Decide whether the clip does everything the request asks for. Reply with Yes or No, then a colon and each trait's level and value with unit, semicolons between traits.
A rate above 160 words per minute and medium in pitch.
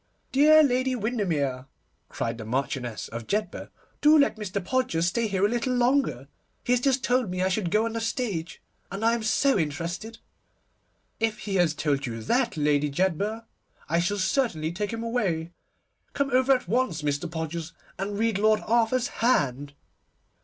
No: average, 170 wpm; high, 205 Hz